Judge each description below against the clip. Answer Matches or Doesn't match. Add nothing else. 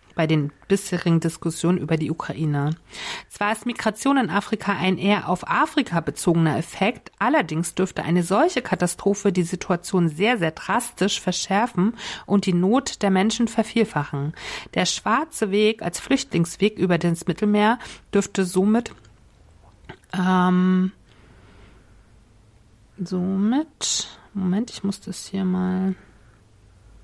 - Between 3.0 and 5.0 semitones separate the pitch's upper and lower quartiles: Matches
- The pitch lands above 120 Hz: Matches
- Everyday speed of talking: Doesn't match